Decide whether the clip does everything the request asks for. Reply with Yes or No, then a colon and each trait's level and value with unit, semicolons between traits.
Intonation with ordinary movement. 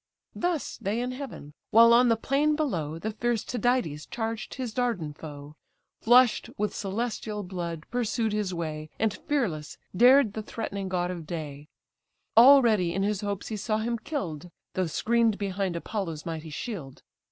No: wide, 5.9 semitones